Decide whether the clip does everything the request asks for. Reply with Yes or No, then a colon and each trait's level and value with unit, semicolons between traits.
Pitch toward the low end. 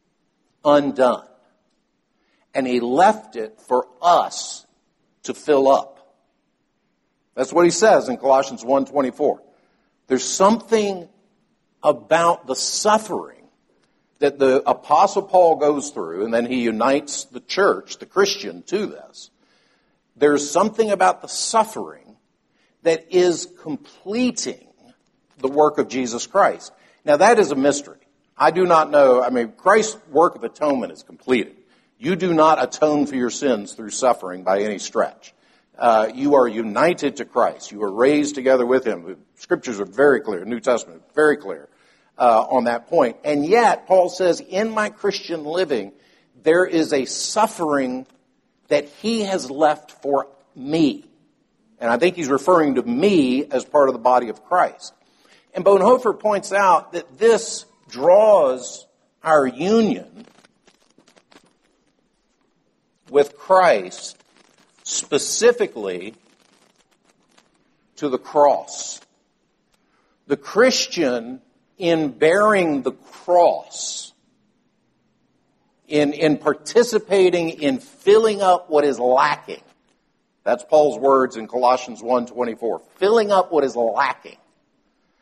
No: medium, 155 Hz